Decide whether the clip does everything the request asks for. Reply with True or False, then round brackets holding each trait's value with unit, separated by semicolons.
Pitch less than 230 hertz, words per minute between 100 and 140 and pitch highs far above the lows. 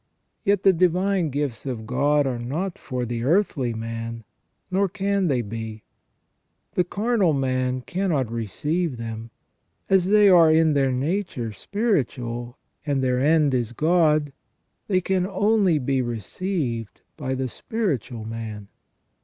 True (140 Hz; 135 wpm; 7.4 semitones)